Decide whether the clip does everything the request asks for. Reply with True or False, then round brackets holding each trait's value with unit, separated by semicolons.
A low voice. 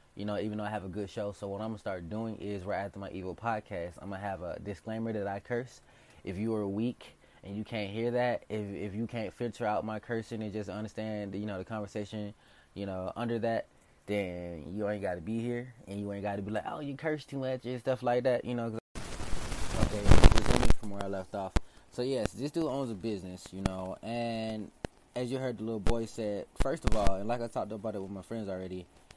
True (105 Hz)